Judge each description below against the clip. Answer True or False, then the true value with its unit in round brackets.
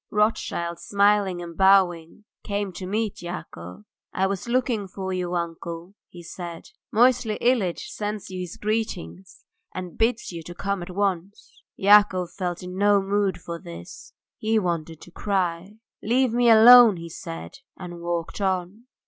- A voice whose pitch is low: False (190 Hz)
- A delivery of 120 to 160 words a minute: True (155 wpm)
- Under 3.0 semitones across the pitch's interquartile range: False (3.3 semitones)